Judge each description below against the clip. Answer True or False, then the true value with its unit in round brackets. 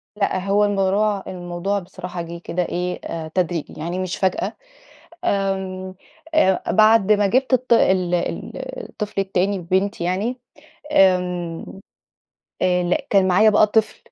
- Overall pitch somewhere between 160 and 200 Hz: True (190 Hz)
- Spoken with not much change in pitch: True (2.3 semitones)